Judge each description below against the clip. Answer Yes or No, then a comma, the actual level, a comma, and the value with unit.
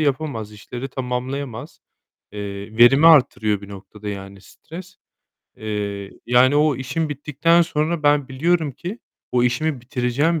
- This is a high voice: No, low, 130 Hz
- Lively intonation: Yes, wide, 5.9 semitones